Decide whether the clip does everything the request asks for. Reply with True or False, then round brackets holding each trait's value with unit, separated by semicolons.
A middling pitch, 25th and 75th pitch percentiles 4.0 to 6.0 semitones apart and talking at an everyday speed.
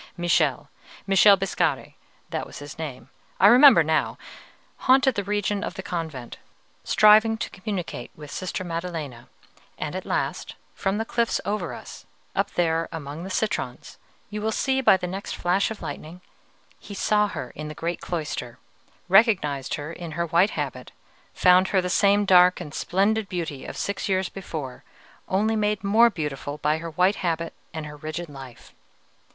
True (180 Hz; 4.6 semitones; 165 wpm)